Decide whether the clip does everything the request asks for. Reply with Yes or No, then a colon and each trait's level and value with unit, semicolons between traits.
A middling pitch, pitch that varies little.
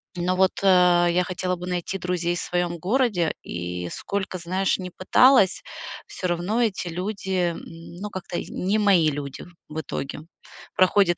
Yes: medium, 180 Hz; narrow, 1.8 semitones